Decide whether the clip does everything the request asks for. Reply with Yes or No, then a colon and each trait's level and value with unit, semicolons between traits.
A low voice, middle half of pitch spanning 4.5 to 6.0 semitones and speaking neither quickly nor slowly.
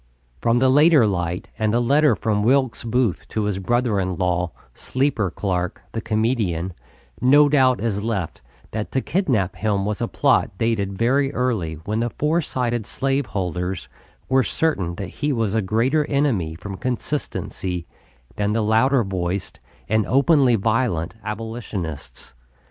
Yes: low, 110 Hz; average, 5.1 semitones; average, 150 wpm